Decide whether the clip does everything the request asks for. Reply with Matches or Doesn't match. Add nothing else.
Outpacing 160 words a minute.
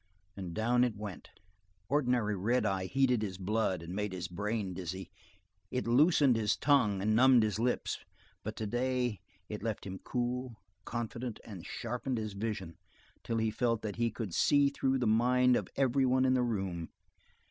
Matches